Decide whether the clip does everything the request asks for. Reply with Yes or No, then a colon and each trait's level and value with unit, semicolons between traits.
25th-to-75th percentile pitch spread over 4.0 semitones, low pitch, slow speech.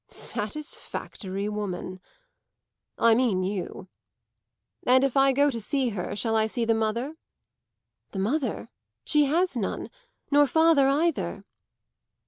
No: average, 5.3 semitones; high, 240 Hz; slow, 120 wpm